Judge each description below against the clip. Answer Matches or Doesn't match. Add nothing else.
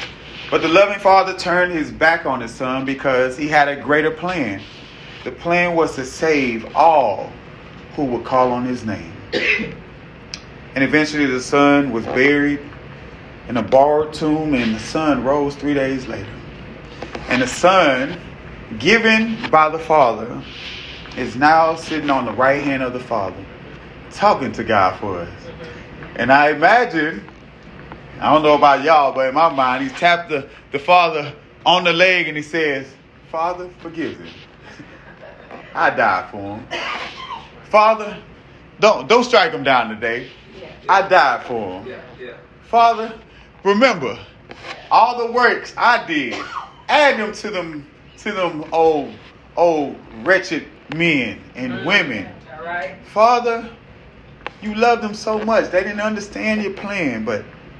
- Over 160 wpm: Doesn't match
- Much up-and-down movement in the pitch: Matches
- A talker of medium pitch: Matches